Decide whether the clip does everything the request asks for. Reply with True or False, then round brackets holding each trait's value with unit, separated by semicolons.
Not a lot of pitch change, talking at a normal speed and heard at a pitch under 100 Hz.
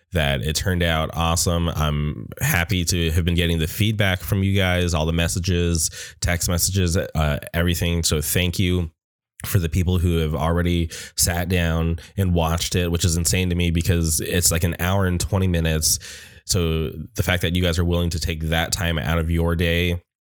True (1.6 semitones; 195 wpm; 85 Hz)